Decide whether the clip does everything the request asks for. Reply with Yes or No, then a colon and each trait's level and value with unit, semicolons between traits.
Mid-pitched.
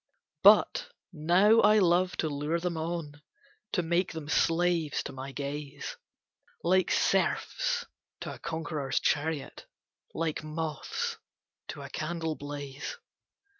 Yes: medium, 160 Hz